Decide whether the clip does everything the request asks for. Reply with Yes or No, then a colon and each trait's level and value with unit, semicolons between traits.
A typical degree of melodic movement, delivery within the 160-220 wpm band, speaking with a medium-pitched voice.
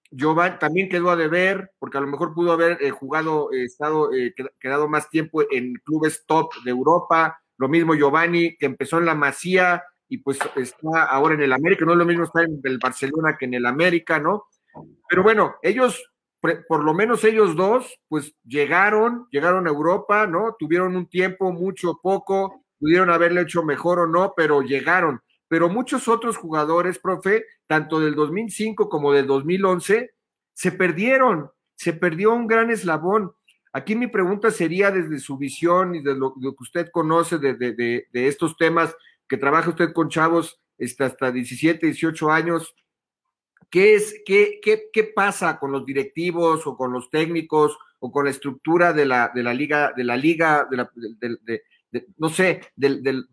Yes: average, 4.5 semitones; average, 185 wpm; medium, 165 Hz